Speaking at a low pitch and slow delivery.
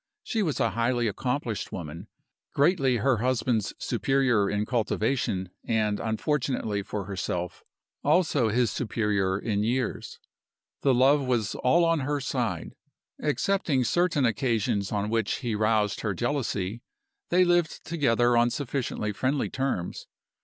Yes: low, 120 Hz; slow, 130 wpm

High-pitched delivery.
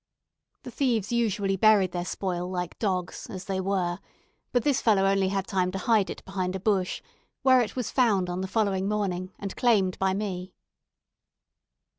Yes: high, 195 Hz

